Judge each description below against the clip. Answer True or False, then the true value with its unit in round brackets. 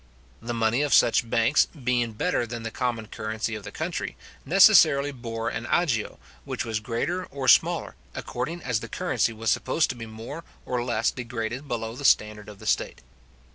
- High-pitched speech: False (115 Hz)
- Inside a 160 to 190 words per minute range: True (180 wpm)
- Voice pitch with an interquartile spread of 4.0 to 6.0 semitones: False (2.6 semitones)